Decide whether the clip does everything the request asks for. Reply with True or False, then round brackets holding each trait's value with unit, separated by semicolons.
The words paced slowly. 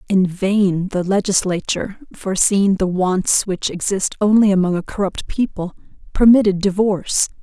True (130 wpm)